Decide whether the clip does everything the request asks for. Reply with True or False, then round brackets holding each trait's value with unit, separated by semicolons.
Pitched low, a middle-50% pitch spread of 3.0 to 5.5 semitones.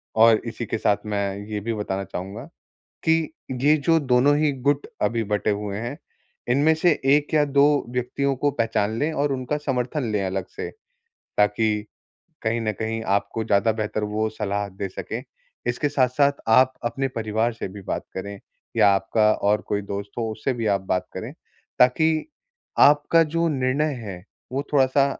True (115 Hz; 5.1 semitones)